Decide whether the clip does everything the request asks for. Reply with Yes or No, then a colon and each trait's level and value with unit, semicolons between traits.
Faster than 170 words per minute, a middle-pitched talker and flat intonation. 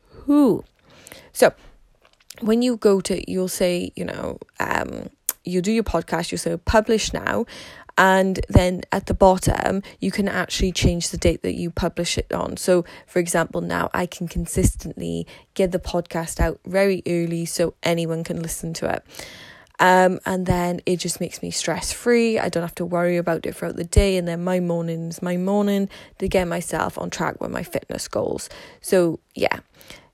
Yes: average, 180 wpm; medium, 180 Hz; narrow, 2.1 semitones